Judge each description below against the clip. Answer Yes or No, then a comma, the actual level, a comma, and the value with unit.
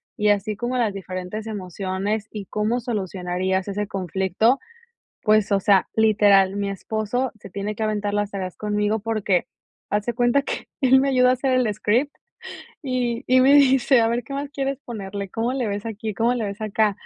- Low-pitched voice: No, high, 215 Hz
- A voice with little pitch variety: No, average, 3.5 semitones